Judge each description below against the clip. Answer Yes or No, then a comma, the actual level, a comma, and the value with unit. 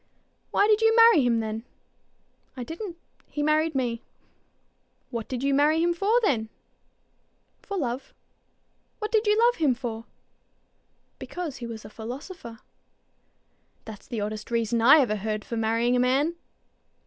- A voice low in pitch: No, very high, 255 Hz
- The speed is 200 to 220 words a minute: No, average, 150 wpm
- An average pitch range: No, wide, 6.8 semitones